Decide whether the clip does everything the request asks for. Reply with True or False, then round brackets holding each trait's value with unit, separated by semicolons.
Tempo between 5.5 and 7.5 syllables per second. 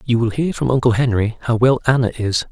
True (5.7 syllables/s)